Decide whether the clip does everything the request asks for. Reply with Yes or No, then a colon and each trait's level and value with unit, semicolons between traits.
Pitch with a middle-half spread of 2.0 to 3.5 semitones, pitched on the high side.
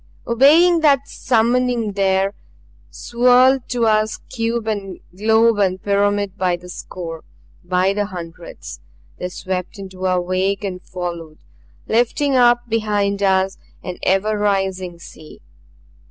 No: average, 3.9 semitones; high, 200 Hz